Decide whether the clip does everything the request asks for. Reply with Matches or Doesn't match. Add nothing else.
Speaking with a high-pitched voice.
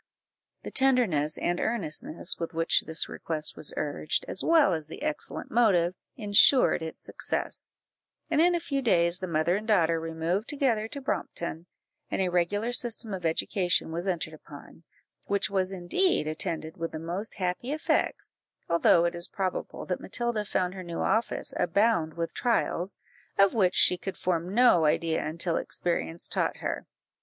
Doesn't match